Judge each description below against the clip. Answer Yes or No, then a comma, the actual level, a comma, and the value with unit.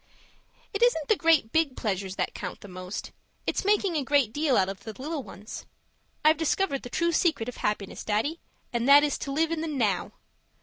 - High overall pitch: Yes, very high, 280 Hz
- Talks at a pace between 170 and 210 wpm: Yes, fast, 205 wpm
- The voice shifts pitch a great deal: Yes, wide, 7.3 semitones